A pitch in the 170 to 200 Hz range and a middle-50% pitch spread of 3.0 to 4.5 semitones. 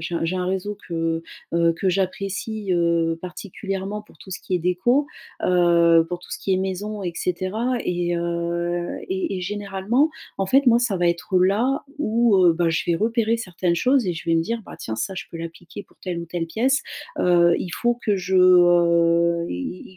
Yes: medium, 185 Hz; average, 3.3 semitones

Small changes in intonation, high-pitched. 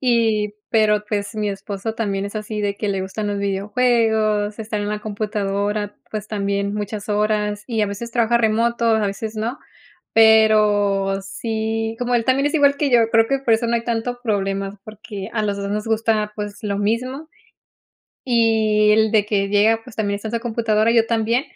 Yes: narrow, 1.7 semitones; high, 215 Hz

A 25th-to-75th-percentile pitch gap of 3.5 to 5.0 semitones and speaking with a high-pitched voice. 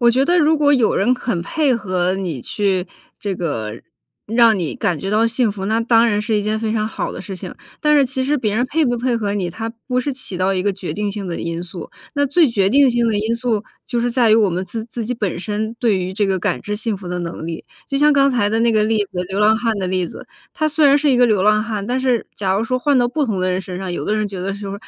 Yes: average, 4.2 semitones; high, 215 Hz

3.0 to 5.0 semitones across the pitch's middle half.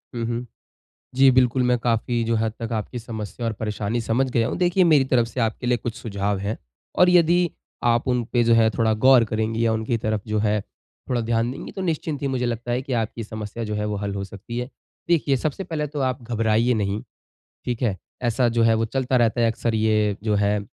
No: narrow, 2.5 semitones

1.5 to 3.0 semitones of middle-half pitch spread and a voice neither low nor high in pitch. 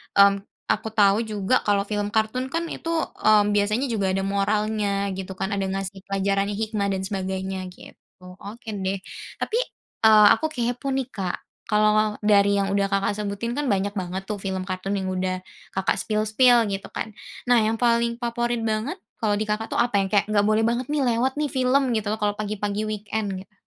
No: narrow, 2.6 semitones; high, 210 Hz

